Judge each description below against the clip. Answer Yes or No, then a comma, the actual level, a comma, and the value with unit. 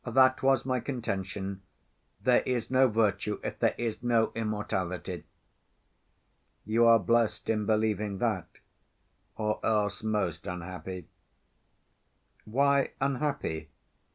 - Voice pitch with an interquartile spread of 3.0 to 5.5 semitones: Yes, average, 3.8 semitones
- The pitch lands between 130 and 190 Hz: No, low, 110 Hz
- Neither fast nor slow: No, slow, 105 wpm